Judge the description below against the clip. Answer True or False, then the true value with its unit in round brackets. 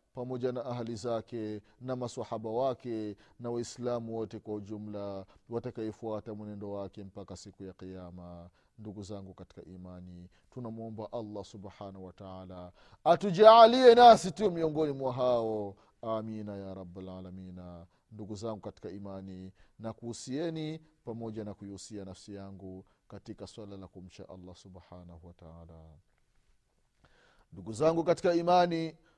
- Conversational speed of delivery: True (115 wpm)